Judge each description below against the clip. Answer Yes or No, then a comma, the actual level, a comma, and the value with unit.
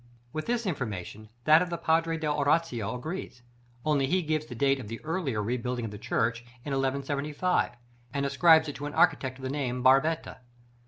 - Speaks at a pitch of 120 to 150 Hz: Yes, medium, 140 Hz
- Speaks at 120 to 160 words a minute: No, average, 195 wpm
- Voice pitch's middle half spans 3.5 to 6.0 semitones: Yes, average, 4.2 semitones